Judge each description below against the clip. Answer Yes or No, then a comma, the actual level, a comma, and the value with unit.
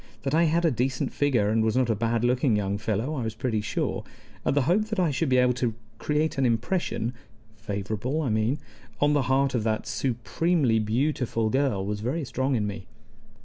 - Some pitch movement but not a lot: Yes, average, 4.4 semitones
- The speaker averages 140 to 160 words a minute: No, fast, 205 wpm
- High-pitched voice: No, low, 125 Hz